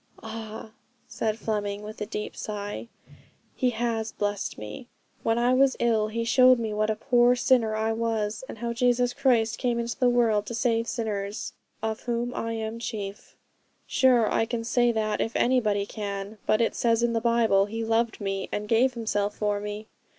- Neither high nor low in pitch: No, high, 225 Hz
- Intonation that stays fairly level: Yes, narrow, 2.1 semitones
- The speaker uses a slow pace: No, average, 185 wpm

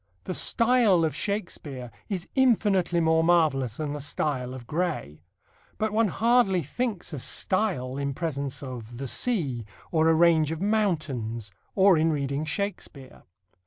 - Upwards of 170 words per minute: No, average, 145 wpm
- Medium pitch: Yes, medium, 160 Hz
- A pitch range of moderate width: No, wide, 6.3 semitones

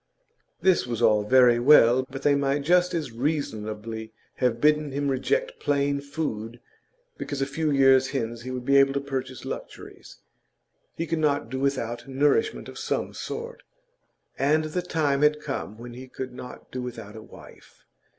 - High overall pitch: No, low, 135 Hz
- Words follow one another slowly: No, average, 170 wpm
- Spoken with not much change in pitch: No, average, 3.5 semitones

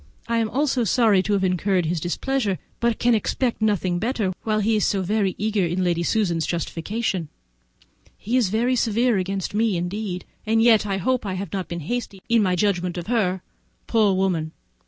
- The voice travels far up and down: No, average, 3.7 semitones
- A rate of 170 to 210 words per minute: Yes, average, 185 wpm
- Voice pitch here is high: Yes, high, 200 Hz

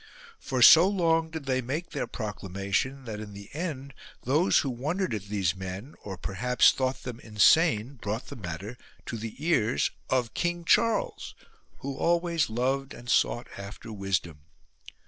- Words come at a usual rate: Yes, average, 155 wpm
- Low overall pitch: Yes, low, 125 Hz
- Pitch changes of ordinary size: No, wide, 6.7 semitones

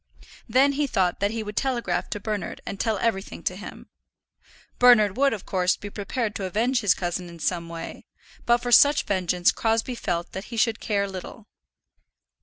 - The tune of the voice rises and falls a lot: No, average, 4.3 semitones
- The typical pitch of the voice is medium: No, high, 210 Hz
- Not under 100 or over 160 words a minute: No, average, 185 wpm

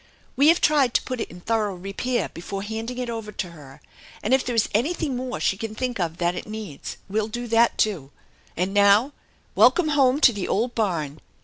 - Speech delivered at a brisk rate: Yes, fast, 210 wpm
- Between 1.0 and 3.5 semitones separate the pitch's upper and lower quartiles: No, average, 4.4 semitones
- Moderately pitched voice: No, high, 220 Hz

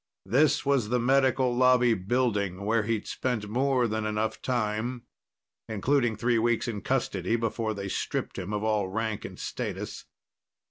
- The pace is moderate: Yes, average, 150 wpm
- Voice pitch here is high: No, low, 115 Hz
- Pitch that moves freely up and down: No, average, 2.9 semitones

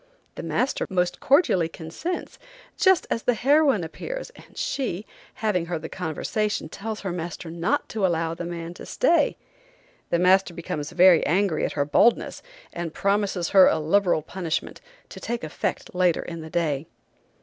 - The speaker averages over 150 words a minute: Yes, average, 160 wpm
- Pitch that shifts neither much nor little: Yes, average, 4.1 semitones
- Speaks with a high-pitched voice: No, medium, 180 Hz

